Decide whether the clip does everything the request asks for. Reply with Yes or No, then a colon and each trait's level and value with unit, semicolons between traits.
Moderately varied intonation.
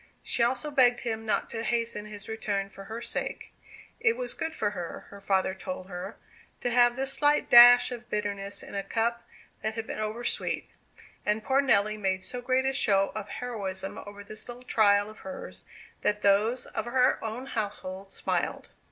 Yes: average, 3.4 semitones